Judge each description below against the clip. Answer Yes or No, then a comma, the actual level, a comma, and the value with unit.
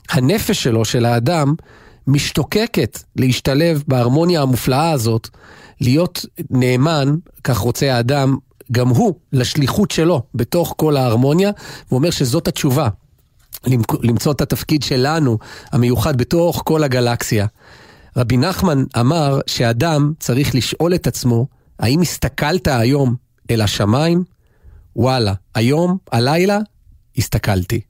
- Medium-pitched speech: No, low, 130 Hz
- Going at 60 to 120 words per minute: Yes, average, 105 wpm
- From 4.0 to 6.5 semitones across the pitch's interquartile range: Yes, average, 4.8 semitones